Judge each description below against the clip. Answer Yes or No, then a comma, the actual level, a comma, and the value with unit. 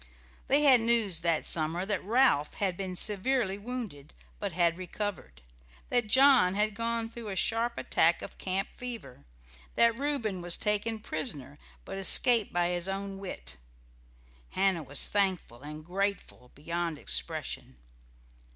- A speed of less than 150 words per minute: Yes, average, 140 wpm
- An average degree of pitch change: Yes, average, 4.9 semitones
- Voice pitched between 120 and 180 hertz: No, high, 195 Hz